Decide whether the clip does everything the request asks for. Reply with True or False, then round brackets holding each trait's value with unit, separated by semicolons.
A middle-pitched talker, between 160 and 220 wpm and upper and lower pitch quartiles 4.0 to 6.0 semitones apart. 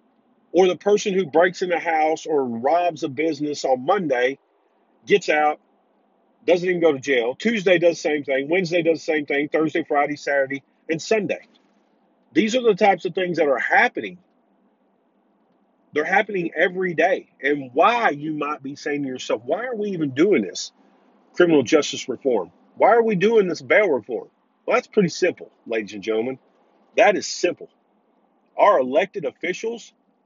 True (165 Hz; 170 wpm; 5.5 semitones)